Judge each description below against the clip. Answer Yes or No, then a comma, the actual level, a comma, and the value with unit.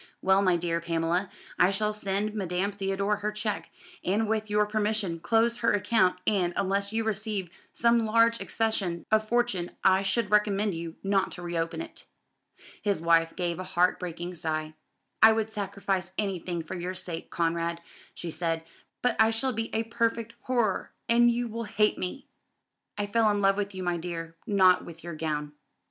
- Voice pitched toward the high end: Yes, high, 195 Hz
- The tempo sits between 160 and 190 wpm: Yes, average, 175 wpm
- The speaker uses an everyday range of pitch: Yes, average, 3.8 semitones